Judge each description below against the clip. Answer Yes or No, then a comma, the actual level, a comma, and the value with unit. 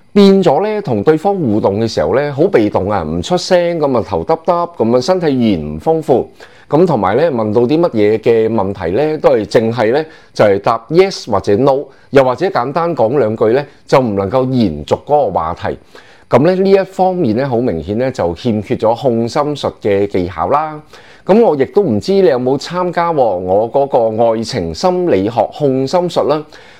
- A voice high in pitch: No, low, 135 Hz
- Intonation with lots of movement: Yes, wide, 7.5 semitones